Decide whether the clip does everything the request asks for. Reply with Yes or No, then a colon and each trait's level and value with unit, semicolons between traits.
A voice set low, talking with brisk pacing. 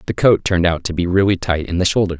Yes: very low, 90 Hz; fast, 330 wpm